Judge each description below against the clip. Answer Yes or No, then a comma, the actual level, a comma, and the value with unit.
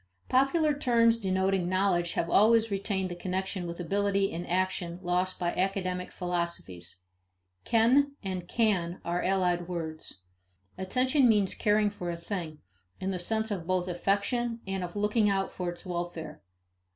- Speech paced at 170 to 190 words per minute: No, average, 150 wpm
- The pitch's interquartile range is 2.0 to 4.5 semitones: Yes, average, 3.0 semitones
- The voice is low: No, medium, 185 Hz